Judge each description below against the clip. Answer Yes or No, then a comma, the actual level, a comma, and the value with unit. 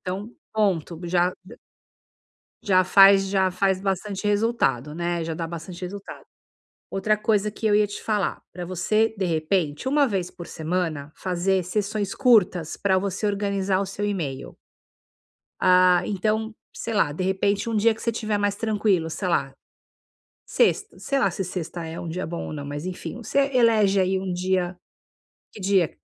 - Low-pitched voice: No, high, 190 Hz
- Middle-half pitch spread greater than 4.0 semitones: No, average, 2.9 semitones